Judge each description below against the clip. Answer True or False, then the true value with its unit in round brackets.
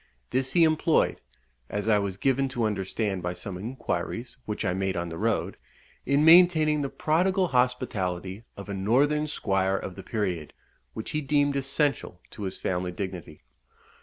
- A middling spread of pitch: False (7.1 semitones)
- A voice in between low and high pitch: False (110 Hz)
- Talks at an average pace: True (165 wpm)